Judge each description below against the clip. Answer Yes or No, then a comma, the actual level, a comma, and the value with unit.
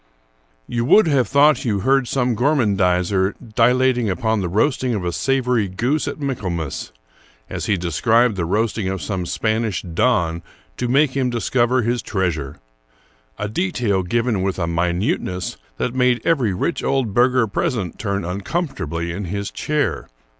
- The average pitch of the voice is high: No, low, 110 Hz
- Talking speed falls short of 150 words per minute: No, average, 155 wpm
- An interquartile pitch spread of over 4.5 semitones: Yes, wide, 5.5 semitones